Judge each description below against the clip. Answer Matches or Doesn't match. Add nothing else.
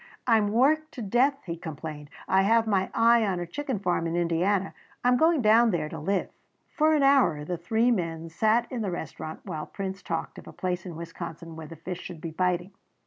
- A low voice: Doesn't match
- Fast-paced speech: Matches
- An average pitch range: Doesn't match